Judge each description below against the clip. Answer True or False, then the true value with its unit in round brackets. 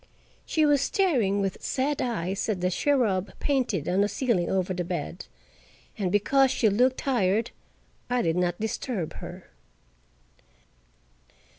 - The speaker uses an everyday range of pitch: False (6.0 semitones)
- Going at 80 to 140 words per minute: True (135 wpm)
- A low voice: False (205 Hz)